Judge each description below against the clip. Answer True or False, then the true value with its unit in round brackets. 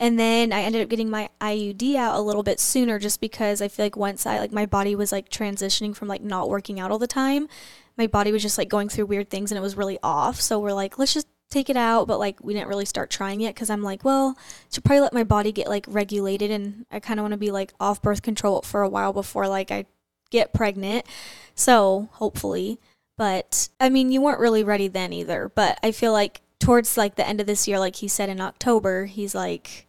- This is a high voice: True (210 Hz)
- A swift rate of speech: True (250 wpm)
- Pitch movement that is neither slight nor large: False (2.1 semitones)